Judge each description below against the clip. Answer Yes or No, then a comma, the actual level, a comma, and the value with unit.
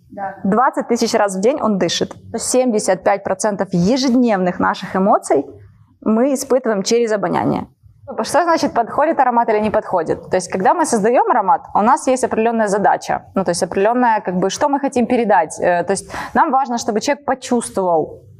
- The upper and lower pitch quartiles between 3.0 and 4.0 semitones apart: No, average, 4.5 semitones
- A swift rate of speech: Yes, fast, 165 wpm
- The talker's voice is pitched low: No, high, 225 Hz